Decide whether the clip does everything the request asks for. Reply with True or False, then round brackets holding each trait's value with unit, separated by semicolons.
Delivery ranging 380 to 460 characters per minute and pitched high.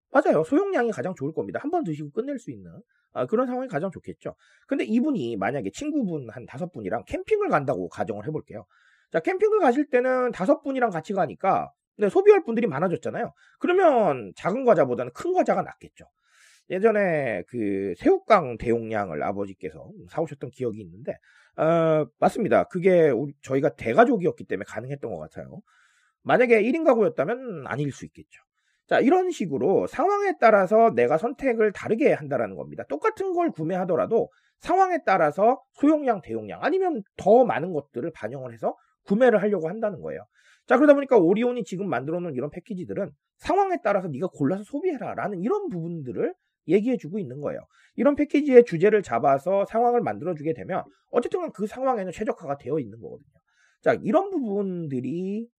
True (390 characters per minute; 215 Hz)